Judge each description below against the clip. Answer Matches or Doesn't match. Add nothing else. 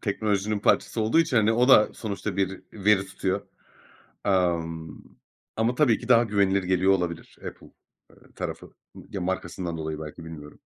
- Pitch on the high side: Doesn't match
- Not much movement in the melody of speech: Doesn't match